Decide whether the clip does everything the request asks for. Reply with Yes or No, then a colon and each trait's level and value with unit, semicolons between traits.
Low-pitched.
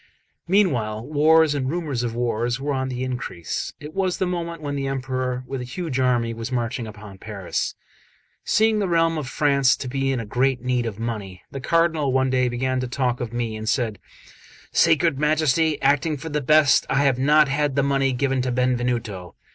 Yes: low, 130 Hz